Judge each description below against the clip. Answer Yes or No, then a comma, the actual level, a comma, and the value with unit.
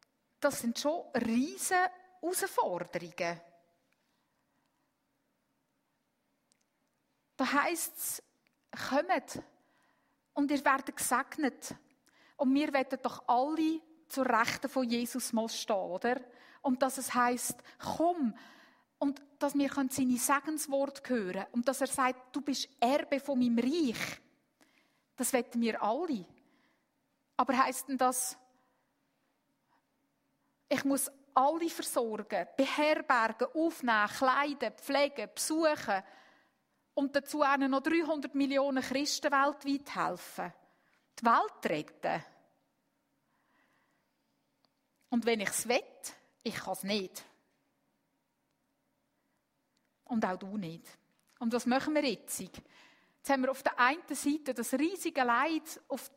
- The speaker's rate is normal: No, slow, 110 wpm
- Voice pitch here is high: Yes, very high, 270 Hz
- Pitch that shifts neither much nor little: Yes, average, 3.0 semitones